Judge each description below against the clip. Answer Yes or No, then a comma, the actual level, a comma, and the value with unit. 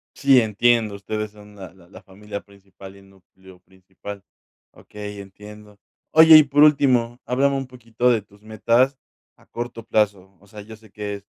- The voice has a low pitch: Yes, low, 105 Hz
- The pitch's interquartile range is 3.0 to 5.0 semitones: Yes, average, 3.3 semitones